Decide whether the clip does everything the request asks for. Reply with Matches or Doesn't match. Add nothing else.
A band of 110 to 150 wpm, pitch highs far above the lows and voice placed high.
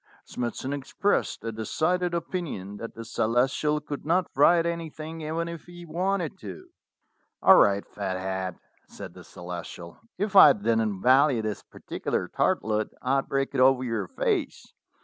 Doesn't match